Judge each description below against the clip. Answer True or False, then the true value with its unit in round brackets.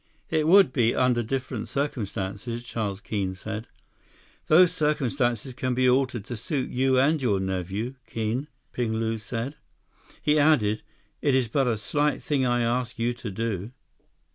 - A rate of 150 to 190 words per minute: True (155 wpm)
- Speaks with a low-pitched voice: True (120 Hz)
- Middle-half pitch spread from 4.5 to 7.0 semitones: False (3.5 semitones)